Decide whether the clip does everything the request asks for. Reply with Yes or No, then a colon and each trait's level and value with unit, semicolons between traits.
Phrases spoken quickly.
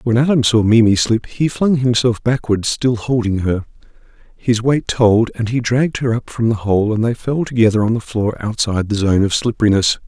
Yes: fast, 210 wpm